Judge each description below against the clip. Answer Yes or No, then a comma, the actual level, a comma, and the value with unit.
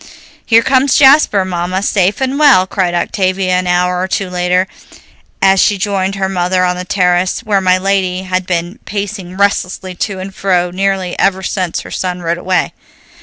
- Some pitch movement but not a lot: No, narrow, 1.5 semitones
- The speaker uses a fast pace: No, average, 175 wpm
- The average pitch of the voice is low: No, medium, 185 Hz